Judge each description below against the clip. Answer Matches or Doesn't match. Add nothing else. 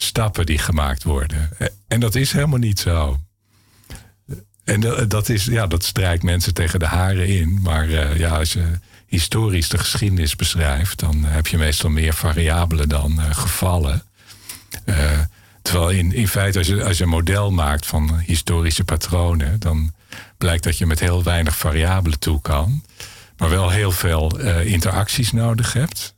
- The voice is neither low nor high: Doesn't match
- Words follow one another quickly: Doesn't match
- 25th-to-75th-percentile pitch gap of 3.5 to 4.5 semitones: Matches